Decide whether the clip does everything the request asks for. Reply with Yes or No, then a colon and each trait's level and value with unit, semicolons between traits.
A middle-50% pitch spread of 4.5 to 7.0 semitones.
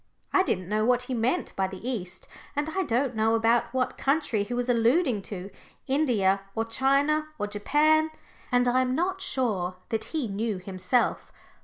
Yes: average, 4.9 semitones